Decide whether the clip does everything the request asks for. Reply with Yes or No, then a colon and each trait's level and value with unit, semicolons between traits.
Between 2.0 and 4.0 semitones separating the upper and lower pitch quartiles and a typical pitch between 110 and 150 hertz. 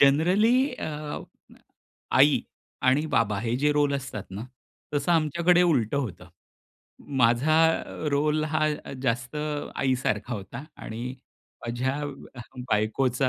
No: average, 4.6 semitones; medium, 140 Hz